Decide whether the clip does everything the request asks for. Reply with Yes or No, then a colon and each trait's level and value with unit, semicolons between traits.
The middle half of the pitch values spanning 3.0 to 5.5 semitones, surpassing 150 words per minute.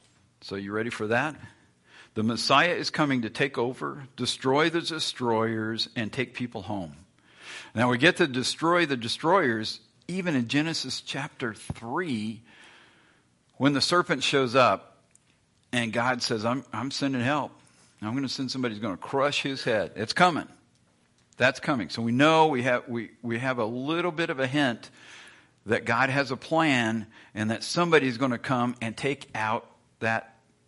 Yes: average, 3.7 semitones; average, 170 wpm